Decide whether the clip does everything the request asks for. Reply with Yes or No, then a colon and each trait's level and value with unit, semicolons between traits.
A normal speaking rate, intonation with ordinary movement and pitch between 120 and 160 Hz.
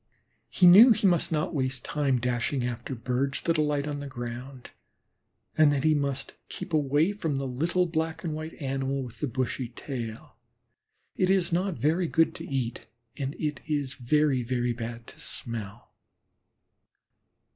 Yes: average, 160 wpm; average, 4.0 semitones; medium, 140 Hz